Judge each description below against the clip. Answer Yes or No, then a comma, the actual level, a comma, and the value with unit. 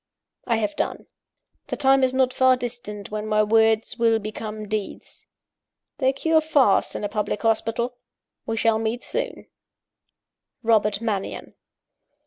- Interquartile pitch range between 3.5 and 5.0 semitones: No, average, 2.8 semitones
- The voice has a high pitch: Yes, high, 225 Hz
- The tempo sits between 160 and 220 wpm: No, slow, 135 wpm